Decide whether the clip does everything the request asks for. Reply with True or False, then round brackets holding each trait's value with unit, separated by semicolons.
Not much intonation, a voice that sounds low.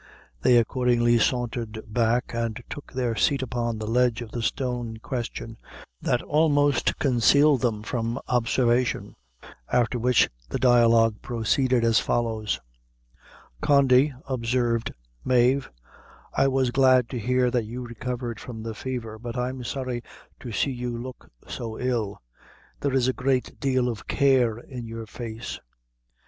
True (1.9 semitones; 120 Hz)